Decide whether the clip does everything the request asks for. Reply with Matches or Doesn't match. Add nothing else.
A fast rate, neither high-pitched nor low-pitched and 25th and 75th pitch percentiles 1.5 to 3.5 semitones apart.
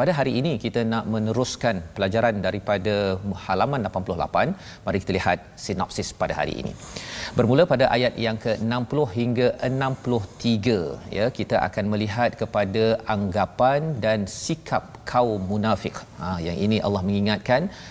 Doesn't match